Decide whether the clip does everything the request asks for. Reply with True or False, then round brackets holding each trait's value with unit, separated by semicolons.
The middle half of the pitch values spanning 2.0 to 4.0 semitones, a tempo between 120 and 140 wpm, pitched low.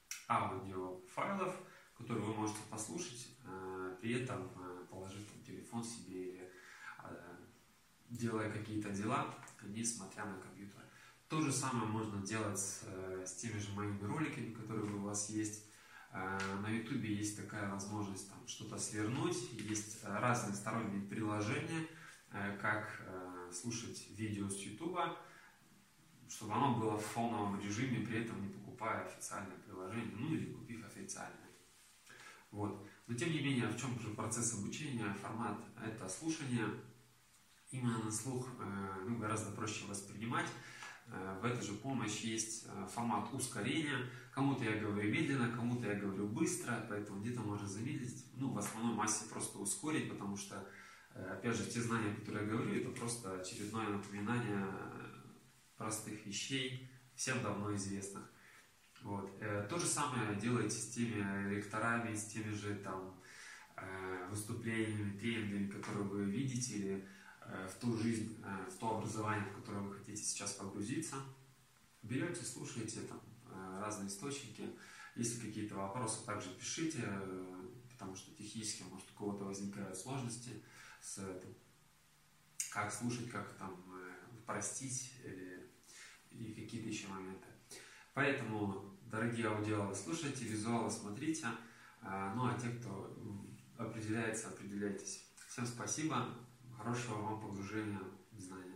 True (3.0 semitones; 125 wpm; 110 Hz)